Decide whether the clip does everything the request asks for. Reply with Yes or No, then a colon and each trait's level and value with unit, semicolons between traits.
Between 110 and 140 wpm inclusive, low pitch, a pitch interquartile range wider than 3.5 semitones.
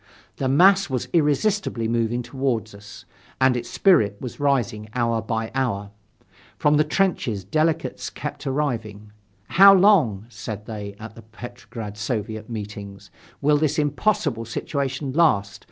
Yes: slow, 135 wpm; low, 120 Hz; wide, 5.4 semitones